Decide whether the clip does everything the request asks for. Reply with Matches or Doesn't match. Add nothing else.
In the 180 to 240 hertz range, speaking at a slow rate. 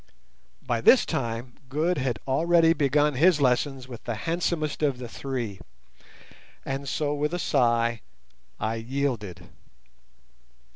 Doesn't match